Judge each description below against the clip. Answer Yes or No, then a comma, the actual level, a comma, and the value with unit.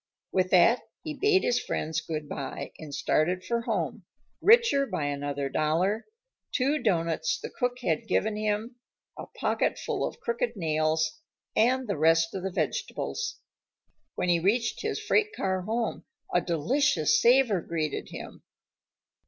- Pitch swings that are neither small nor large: No, wide, 7.6 semitones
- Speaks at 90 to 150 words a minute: Yes, average, 145 wpm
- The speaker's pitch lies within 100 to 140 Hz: No, high, 190 Hz